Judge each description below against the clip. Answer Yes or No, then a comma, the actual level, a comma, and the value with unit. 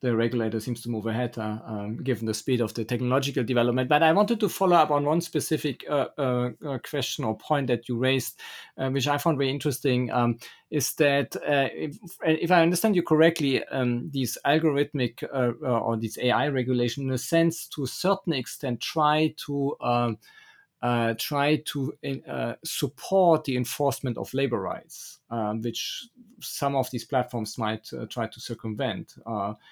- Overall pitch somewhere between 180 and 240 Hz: No, low, 135 Hz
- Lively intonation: No, average, 4.1 semitones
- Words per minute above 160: Yes, average, 180 wpm